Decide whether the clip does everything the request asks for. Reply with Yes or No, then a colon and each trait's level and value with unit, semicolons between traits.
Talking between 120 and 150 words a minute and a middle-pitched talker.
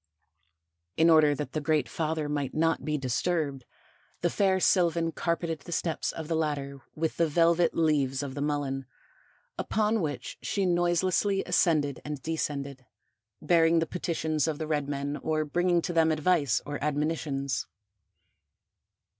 Yes: average, 145 wpm; medium, 155 Hz